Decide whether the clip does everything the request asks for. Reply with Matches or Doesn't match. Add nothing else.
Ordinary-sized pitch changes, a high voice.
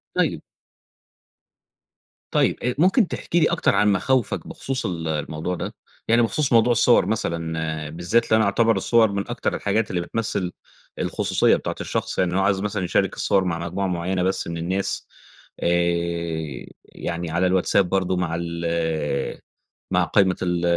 Doesn't match